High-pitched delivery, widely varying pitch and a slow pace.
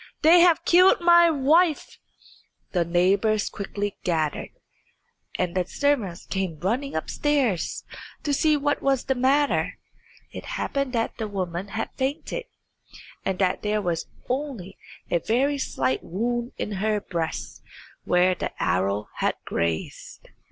Yes: high, 215 Hz; wide, 7.8 semitones; slow, 130 wpm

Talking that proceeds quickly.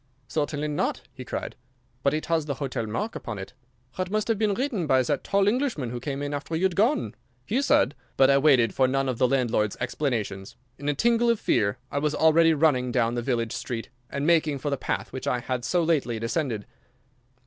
Yes: fast, 220 wpm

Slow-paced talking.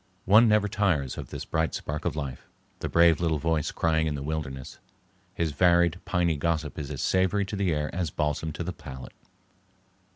No: average, 190 wpm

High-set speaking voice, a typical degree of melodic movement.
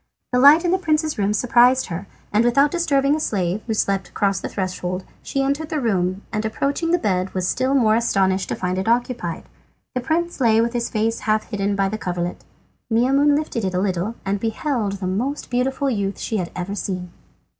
No: high, 220 Hz; wide, 5.8 semitones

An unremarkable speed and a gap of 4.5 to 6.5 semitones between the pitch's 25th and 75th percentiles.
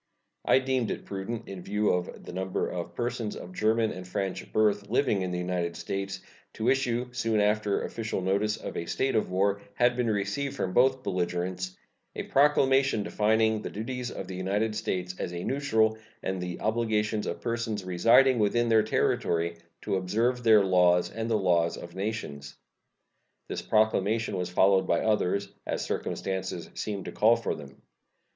No: average, 170 wpm; average, 3.7 semitones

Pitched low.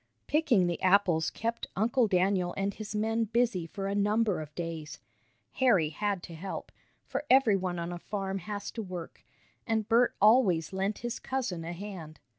No: high, 195 Hz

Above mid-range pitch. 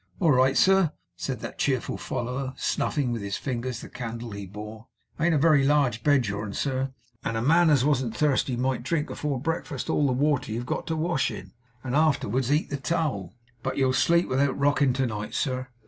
No: low, 130 Hz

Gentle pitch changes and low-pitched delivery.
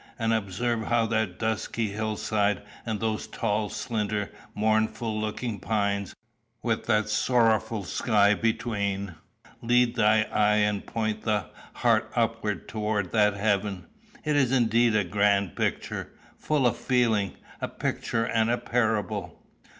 Yes: narrow, 1.8 semitones; low, 110 Hz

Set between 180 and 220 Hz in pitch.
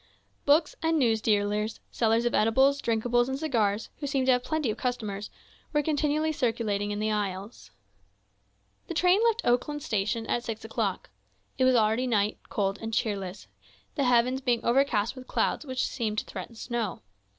No: high, 235 Hz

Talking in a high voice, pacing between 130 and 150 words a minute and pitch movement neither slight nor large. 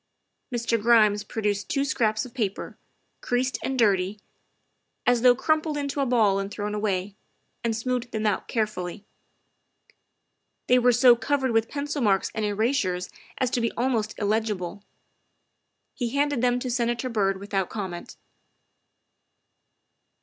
Yes: high, 225 Hz; slow, 135 wpm; average, 3.4 semitones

